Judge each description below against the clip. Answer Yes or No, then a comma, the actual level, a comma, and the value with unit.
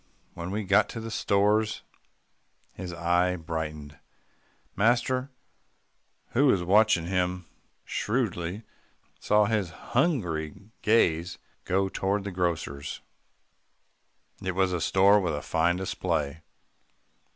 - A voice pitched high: No, very low, 95 Hz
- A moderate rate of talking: No, slow, 105 wpm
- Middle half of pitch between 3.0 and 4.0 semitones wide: Yes, average, 3.7 semitones